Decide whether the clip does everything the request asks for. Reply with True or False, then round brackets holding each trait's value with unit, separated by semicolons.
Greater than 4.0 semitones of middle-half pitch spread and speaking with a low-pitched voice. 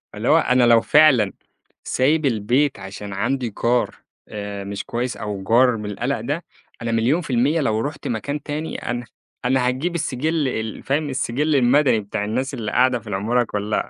True (4.4 semitones; 125 Hz)